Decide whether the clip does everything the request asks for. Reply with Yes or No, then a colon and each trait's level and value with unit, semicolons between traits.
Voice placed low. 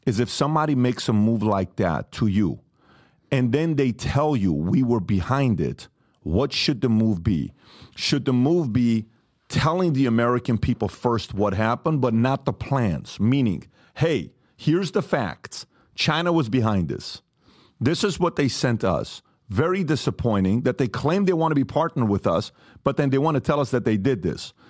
Yes: low, 130 Hz